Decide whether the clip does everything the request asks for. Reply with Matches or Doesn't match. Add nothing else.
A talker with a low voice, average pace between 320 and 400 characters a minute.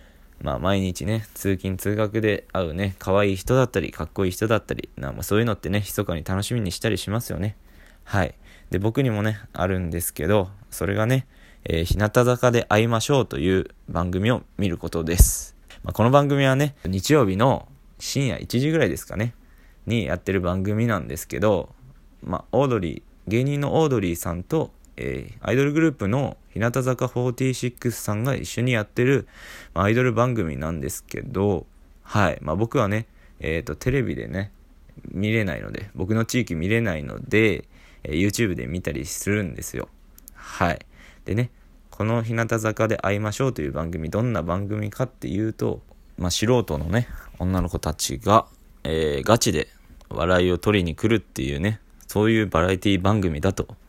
Matches